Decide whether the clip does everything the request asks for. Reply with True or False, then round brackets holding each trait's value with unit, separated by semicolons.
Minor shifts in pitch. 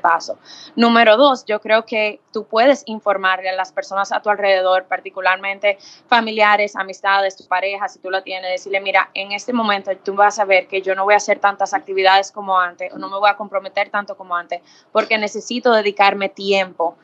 True (1.8 semitones)